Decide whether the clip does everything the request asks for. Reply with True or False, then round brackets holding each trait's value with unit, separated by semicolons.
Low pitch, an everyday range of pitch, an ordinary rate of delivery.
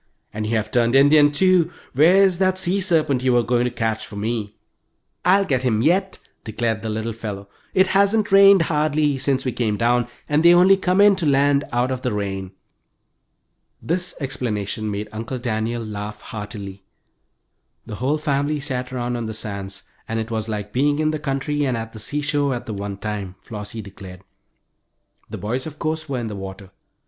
False (125 Hz; 5.8 semitones; 190 wpm)